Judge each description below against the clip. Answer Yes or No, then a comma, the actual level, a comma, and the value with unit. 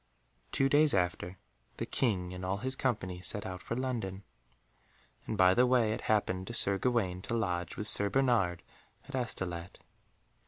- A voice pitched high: No, low, 100 Hz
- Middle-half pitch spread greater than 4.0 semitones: Yes, average, 4.9 semitones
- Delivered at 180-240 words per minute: No, average, 165 wpm